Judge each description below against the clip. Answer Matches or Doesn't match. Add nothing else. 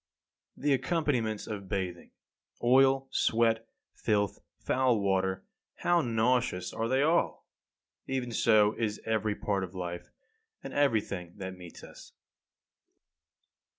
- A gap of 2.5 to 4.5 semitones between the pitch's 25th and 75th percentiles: Doesn't match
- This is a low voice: Matches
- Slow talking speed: Matches